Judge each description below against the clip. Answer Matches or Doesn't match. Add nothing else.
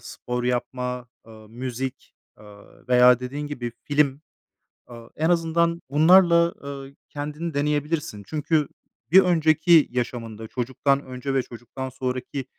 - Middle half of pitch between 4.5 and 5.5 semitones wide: Doesn't match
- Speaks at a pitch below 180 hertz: Matches